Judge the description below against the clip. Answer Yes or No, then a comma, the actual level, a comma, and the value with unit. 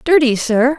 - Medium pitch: No, very high, 265 Hz